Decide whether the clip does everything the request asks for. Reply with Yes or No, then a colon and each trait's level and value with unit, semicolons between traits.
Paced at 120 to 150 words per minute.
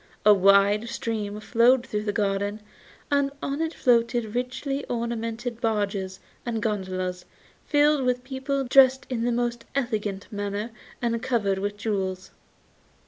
Yes: slow, 135 wpm